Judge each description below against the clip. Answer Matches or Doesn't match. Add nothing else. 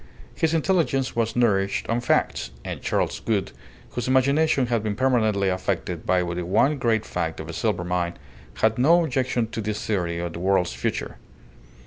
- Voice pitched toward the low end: Matches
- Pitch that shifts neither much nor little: Doesn't match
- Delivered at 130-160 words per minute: Doesn't match